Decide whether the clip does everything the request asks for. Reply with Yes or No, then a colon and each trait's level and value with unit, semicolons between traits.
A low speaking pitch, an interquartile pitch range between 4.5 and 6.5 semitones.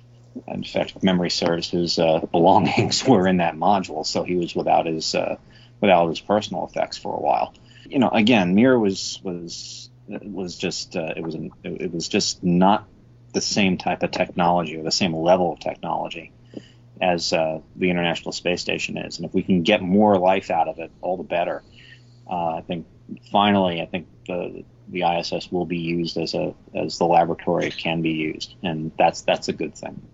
No: very low, 90 Hz; average, 4.0 semitones